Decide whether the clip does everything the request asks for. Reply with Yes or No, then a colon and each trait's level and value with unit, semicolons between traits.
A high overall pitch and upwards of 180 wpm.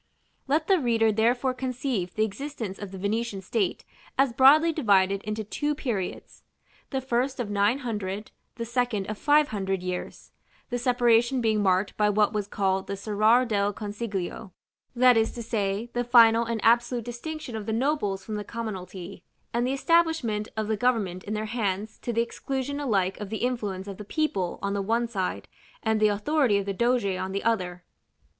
Yes: high, 220 Hz; average, 190 wpm